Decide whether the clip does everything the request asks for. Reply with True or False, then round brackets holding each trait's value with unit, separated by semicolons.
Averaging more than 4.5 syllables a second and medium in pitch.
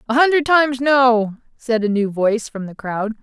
False (5.0 syllables/s; 240 Hz)